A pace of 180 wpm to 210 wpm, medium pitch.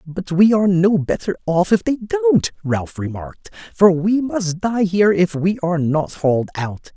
Yes: average, 190 wpm; medium, 175 Hz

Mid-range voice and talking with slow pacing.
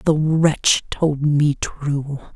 Yes: medium, 150 Hz; slow, 130 wpm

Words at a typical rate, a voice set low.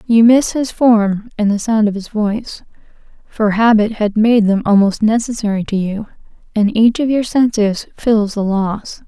No: average, 180 wpm; high, 215 Hz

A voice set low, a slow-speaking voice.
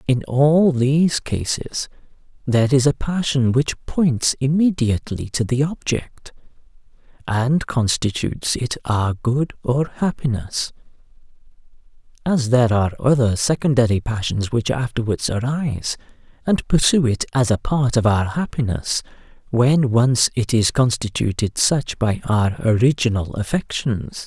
Yes: low, 125 Hz; slow, 120 wpm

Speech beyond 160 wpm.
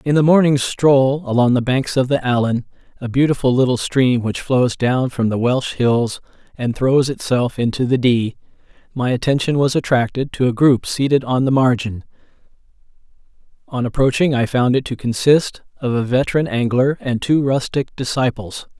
Yes: average, 170 wpm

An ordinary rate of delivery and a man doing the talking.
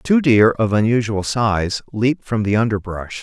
Yes: average, 165 wpm; male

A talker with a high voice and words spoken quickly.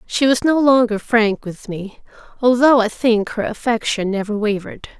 No: high, 225 Hz; average, 170 wpm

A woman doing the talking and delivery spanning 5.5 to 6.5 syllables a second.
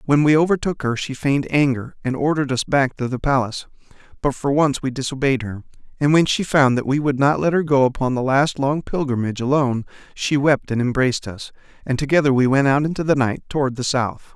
No: male; 6.0 syllables/s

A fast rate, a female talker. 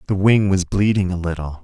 No: fast, 220 wpm; male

